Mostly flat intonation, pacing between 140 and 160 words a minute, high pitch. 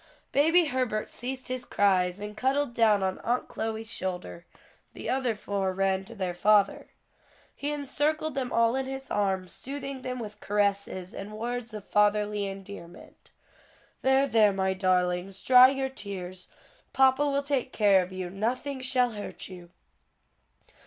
No: average, 5.2 semitones; average, 150 wpm; high, 215 Hz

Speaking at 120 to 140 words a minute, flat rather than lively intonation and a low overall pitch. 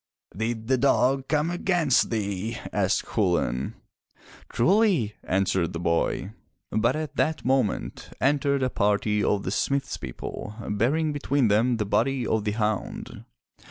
No: slow, 135 wpm; average, 5.2 semitones; low, 115 Hz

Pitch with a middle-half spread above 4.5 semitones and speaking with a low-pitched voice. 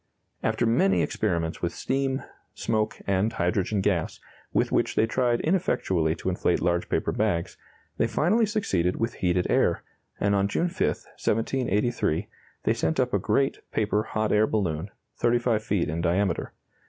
Yes: average, 5.0 semitones; low, 105 Hz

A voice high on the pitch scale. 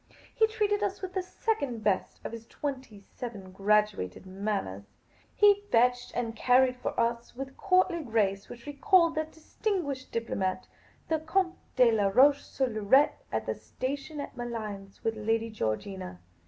Yes: high, 245 Hz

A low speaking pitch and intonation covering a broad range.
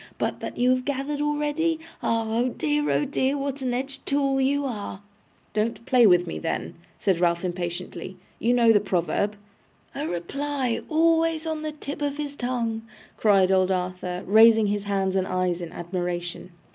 No: high, 230 Hz; wide, 7.3 semitones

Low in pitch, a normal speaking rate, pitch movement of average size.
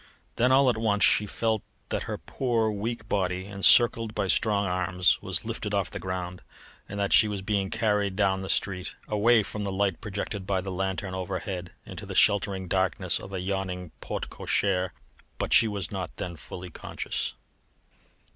No: low, 100 Hz; average, 175 wpm; narrow, 2.3 semitones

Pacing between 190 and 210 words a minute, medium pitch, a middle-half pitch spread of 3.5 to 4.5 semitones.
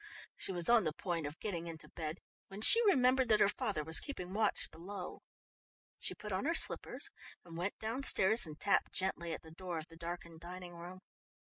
Yes: average, 195 wpm; medium, 180 Hz; average, 4.1 semitones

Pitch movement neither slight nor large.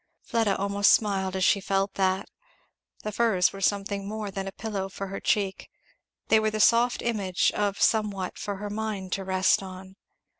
No: narrow, 1.8 semitones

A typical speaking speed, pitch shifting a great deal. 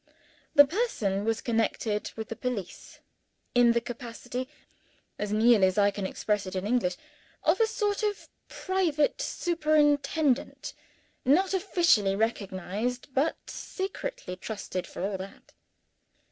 No: slow, 125 wpm; wide, 7.1 semitones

